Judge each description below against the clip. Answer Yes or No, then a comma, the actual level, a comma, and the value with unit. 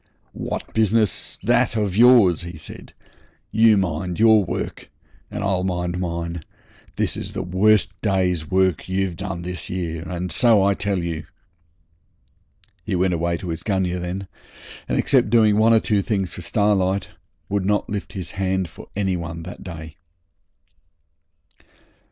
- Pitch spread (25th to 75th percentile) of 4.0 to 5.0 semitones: No, average, 2.8 semitones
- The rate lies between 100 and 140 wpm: No, average, 150 wpm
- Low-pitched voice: Yes, very low, 95 Hz